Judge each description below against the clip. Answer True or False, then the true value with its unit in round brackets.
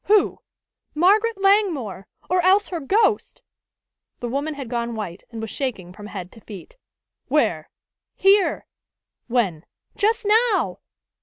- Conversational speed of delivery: False (130 wpm)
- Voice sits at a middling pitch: False (290 Hz)